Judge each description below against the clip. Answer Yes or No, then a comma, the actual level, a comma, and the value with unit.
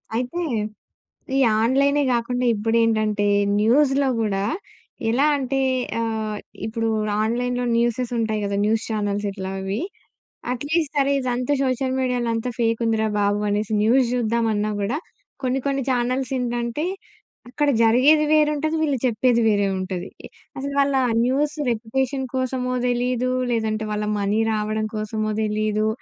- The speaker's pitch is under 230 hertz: No, high, 235 Hz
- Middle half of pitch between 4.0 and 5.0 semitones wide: No, average, 3.3 semitones